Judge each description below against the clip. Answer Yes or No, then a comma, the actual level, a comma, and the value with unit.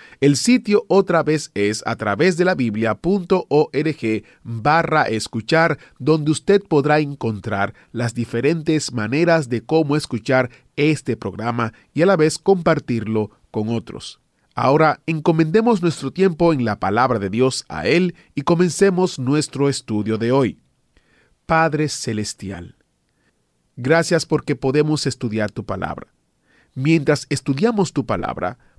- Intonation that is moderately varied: No, wide, 6.0 semitones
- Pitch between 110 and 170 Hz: Yes, medium, 140 Hz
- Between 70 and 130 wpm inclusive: Yes, slow, 125 wpm